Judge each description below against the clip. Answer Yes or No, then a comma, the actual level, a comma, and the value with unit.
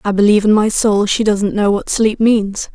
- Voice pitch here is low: No, high, 210 Hz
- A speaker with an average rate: No, fast, 240 wpm